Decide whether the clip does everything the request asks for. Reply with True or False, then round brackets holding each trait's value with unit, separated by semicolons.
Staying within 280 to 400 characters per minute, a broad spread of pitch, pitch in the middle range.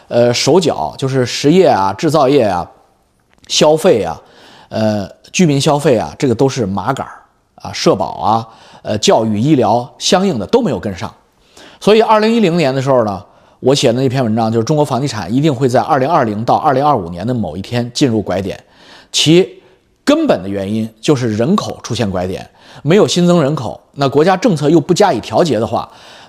False (285 characters per minute; 5.9 semitones; 130 Hz)